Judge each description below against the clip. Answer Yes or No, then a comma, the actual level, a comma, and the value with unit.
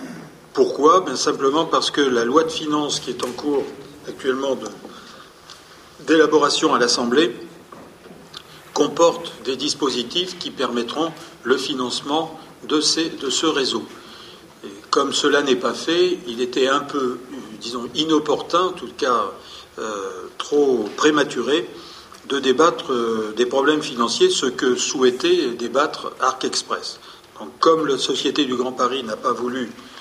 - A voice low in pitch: No, medium, 160 Hz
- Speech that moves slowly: Yes, slow, 140 wpm